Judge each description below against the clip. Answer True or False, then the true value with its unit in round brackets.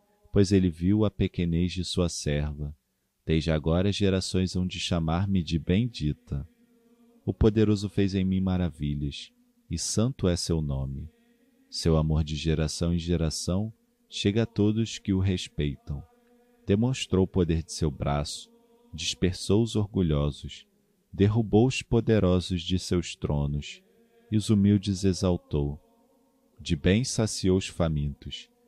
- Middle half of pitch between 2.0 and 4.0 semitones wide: False (5.3 semitones)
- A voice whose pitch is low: True (95 Hz)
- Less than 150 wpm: True (130 wpm)